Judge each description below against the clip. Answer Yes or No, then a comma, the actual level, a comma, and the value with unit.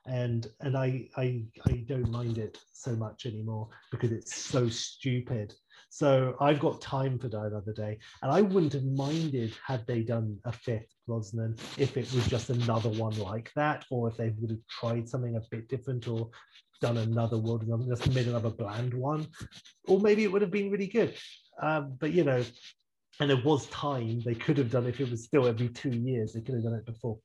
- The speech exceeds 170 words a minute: Yes, fast, 205 wpm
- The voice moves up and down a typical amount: Yes, average, 3.0 semitones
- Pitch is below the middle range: Yes, low, 120 Hz